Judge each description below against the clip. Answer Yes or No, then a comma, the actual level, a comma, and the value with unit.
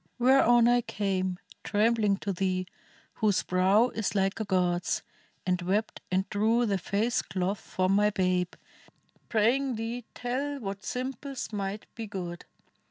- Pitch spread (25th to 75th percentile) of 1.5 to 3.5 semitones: No, average, 3.9 semitones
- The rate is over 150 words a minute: No, average, 140 wpm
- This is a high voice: Yes, high, 205 Hz